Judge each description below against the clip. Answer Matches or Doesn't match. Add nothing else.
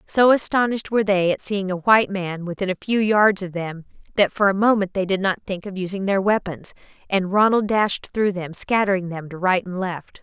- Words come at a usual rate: Doesn't match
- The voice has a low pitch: Doesn't match